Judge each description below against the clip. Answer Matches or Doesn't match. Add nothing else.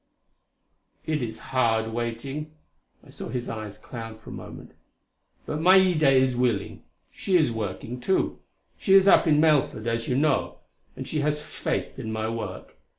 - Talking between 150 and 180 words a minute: Matches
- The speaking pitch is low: Matches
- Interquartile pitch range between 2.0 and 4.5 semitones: Doesn't match